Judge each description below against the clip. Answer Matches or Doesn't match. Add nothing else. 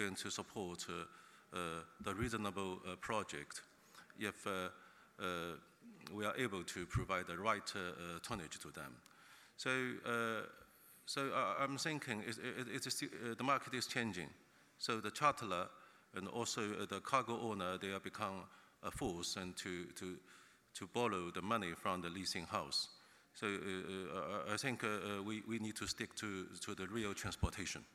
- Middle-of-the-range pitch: Doesn't match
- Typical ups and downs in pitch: Matches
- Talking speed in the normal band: Matches